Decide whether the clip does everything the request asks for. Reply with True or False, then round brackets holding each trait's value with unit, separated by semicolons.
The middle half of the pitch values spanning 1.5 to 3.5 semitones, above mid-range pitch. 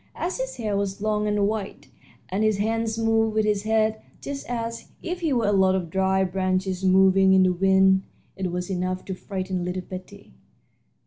True (2.7 semitones; 195 Hz)